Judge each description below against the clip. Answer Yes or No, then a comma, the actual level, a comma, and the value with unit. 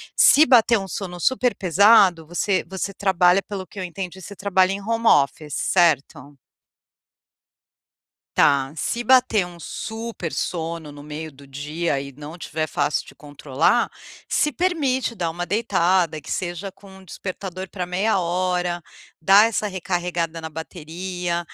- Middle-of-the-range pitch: Yes, medium, 180 Hz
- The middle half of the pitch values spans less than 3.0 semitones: No, average, 3.6 semitones